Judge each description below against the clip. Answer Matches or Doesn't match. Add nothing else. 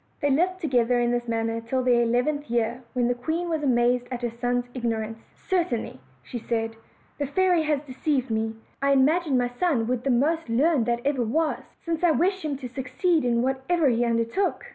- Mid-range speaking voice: Doesn't match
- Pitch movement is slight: Doesn't match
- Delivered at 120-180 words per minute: Doesn't match